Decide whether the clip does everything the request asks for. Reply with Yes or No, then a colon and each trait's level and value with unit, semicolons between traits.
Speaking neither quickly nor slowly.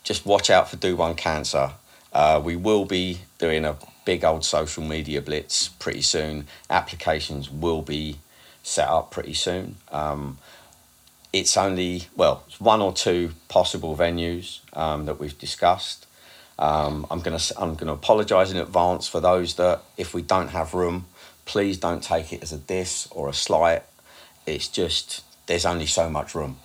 Yes: average, 170 wpm